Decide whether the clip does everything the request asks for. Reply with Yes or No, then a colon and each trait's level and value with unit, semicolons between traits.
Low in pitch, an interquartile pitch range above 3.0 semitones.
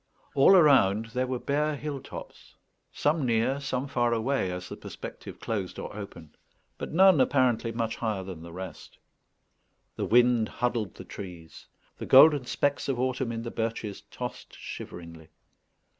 Yes: low, 120 Hz; average, 5.1 semitones